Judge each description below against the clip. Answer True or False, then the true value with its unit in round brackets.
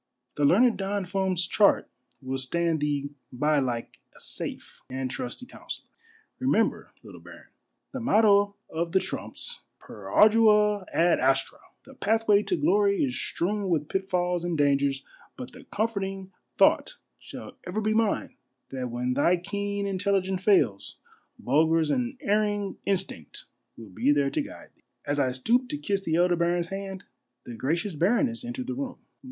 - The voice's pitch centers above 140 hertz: True (190 Hz)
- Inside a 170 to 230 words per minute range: False (160 wpm)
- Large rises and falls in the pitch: True (6.3 semitones)